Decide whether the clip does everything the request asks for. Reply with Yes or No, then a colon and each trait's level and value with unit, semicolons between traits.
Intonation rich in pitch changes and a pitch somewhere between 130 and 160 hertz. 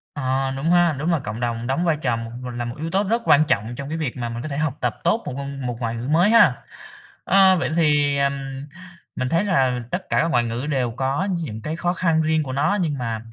No: average, 5.0 semitones; medium, 140 Hz